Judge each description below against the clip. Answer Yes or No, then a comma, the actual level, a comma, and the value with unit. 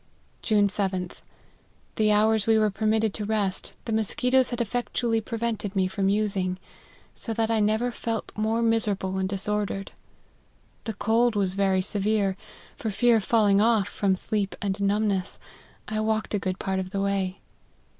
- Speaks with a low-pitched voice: No, high, 210 Hz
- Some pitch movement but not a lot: No, narrow, 2.2 semitones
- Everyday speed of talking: Yes, average, 165 wpm